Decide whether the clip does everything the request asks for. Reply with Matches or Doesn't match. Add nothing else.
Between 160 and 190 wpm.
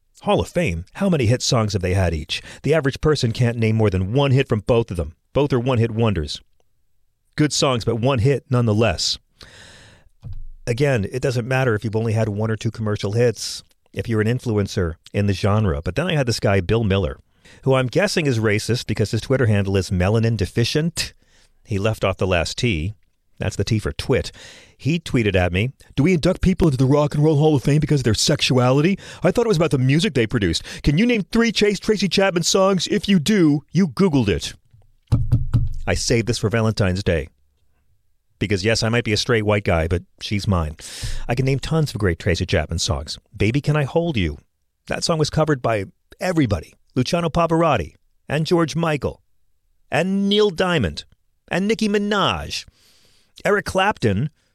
Doesn't match